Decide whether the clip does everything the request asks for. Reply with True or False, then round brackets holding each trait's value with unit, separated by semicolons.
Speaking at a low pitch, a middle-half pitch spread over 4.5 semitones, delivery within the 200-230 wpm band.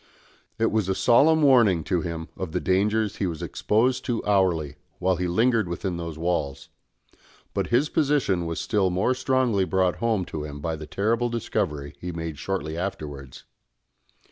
False (95 Hz; 5.5 semitones; 170 wpm)